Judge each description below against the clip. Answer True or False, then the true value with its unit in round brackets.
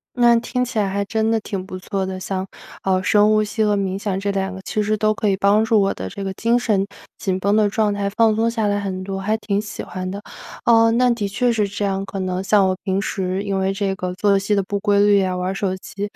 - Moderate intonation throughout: False (1.9 semitones)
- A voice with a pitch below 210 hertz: True (200 Hz)